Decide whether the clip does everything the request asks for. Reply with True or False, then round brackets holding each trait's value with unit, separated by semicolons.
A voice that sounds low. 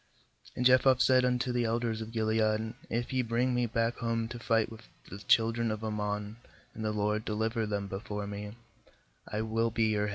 True (110 Hz)